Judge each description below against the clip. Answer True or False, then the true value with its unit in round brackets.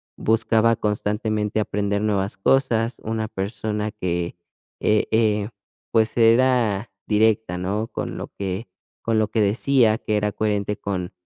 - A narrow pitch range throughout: True (1.7 semitones)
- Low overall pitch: True (105 Hz)